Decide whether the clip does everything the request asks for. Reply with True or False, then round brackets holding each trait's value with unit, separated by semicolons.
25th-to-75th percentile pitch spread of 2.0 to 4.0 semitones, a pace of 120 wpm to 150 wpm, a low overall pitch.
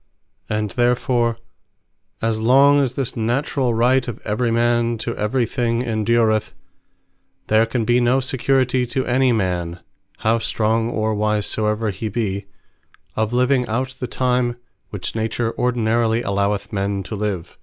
True (2.4 semitones; 145 wpm; 115 Hz)